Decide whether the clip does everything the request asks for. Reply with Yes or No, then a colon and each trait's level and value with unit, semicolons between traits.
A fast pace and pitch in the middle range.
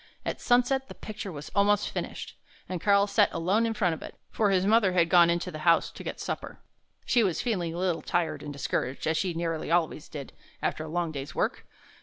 Yes: fast, 220 wpm; medium, 175 Hz